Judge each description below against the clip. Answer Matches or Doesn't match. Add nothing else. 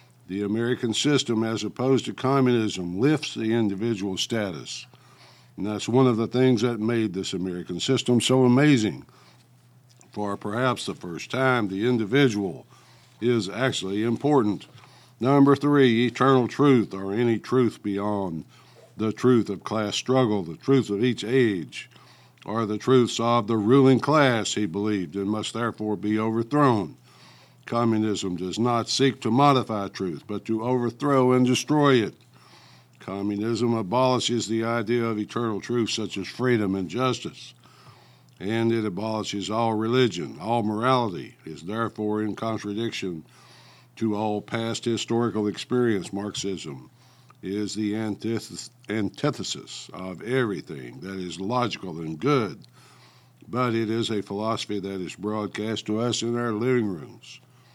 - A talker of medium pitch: Doesn't match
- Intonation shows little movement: Doesn't match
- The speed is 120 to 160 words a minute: Matches